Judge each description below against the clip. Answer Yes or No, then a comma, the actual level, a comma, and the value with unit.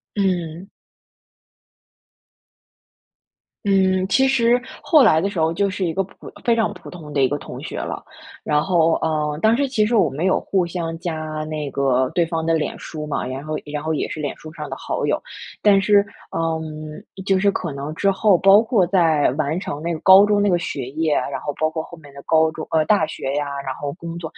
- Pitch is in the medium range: Yes, medium, 165 Hz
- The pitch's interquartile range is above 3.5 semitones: Yes, average, 4.2 semitones